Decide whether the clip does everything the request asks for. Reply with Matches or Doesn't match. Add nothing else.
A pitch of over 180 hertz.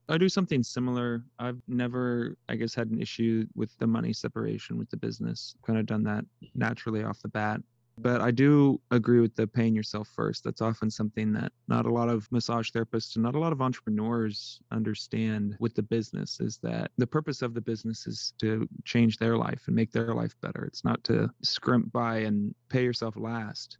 Doesn't match